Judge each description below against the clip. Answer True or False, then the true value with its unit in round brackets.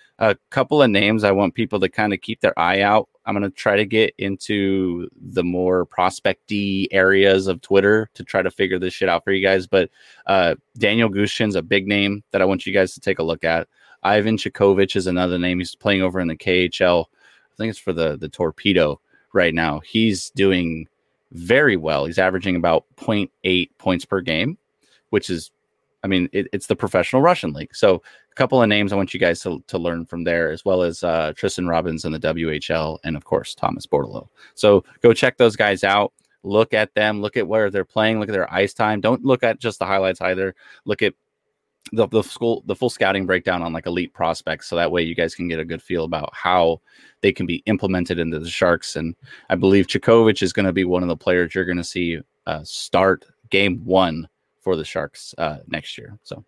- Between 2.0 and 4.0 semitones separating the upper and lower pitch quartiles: True (2.9 semitones)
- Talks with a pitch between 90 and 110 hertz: True (95 Hz)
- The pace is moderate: False (220 wpm)